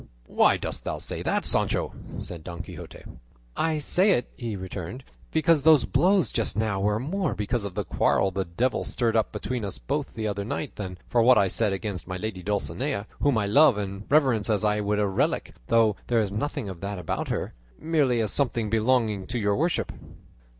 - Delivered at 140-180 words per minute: No, average, 200 wpm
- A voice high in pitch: No, low, 110 Hz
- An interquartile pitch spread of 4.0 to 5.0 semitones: Yes, average, 4.6 semitones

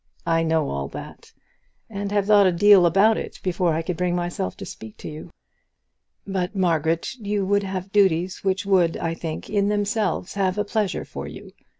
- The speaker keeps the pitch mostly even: No, average, 3.4 semitones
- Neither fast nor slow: Yes, average, 190 wpm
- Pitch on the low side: No, medium, 185 Hz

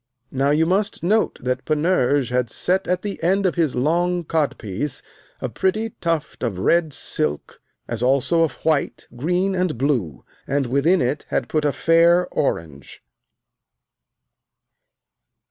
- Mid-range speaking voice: Yes, medium, 155 Hz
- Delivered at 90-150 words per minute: Yes, average, 140 wpm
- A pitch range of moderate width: No, wide, 5.7 semitones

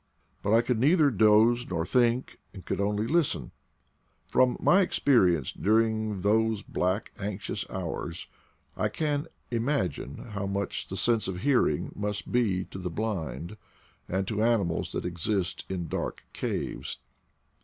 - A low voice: Yes, low, 105 Hz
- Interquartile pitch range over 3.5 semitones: Yes, average, 4.0 semitones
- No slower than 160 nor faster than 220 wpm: No, average, 145 wpm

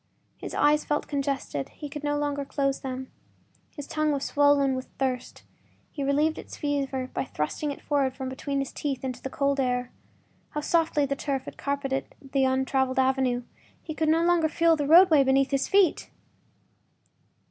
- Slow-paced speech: No, average, 170 wpm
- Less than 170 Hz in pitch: No, very high, 280 Hz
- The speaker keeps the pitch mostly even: Yes, narrow, 1.9 semitones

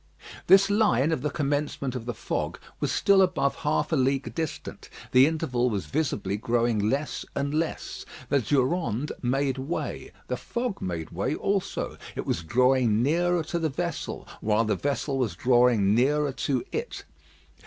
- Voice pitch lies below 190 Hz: Yes, low, 135 Hz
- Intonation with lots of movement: No, average, 4.8 semitones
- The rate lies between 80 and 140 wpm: No, average, 160 wpm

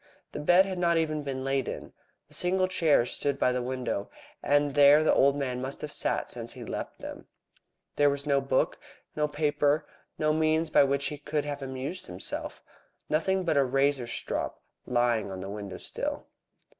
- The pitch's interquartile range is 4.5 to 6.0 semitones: No, average, 2.8 semitones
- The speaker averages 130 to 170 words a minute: No, average, 185 wpm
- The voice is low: No, medium, 145 Hz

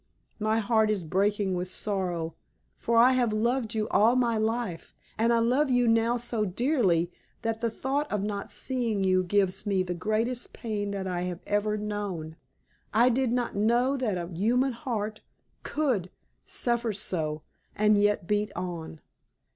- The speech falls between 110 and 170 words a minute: Yes, average, 165 wpm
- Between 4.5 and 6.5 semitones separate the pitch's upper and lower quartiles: No, average, 3.8 semitones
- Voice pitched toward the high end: Yes, high, 215 Hz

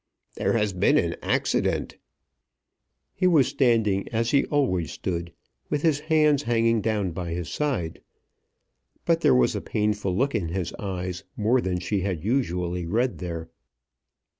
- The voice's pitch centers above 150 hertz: No, low, 105 Hz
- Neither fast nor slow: Yes, average, 150 wpm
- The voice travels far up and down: Yes, wide, 5.8 semitones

